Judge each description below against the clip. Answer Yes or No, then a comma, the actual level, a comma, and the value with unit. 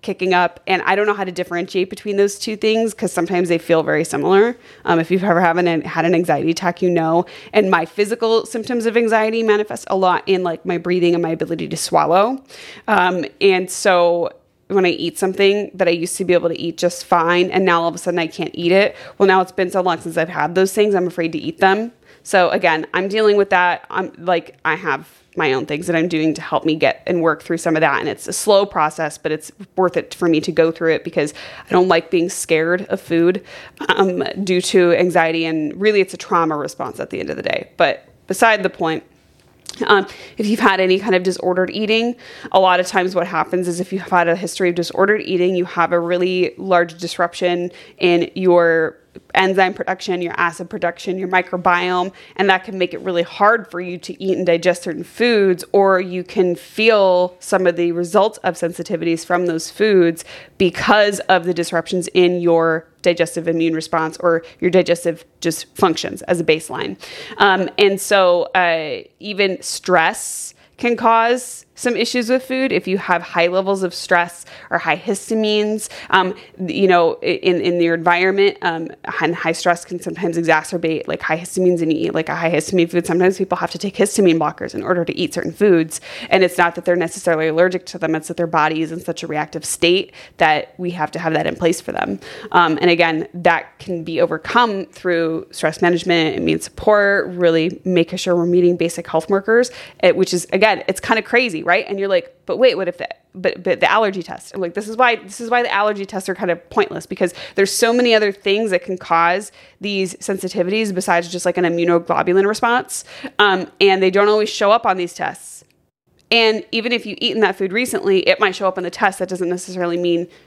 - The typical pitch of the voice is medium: Yes, medium, 180 Hz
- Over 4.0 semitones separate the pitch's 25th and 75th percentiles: No, narrow, 2.4 semitones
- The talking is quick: Yes, fast, 215 wpm